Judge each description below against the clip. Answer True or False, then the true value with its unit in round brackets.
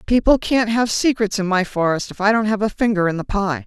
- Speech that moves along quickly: True (260 wpm)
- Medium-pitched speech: False (210 Hz)